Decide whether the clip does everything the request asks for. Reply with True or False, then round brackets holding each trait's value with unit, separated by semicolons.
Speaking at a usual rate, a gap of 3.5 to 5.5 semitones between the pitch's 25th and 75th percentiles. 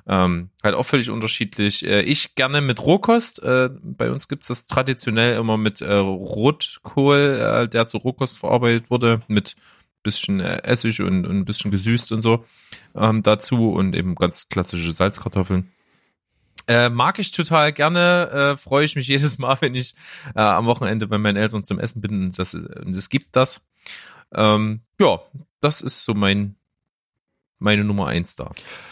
True (165 wpm; 4.8 semitones)